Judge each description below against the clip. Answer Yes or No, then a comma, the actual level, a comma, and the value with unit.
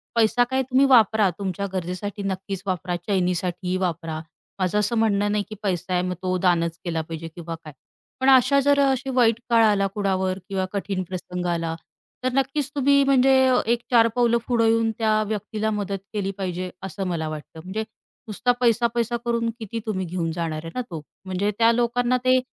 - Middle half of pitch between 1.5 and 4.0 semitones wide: No, average, 4.6 semitones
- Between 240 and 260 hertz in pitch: No, high, 200 Hz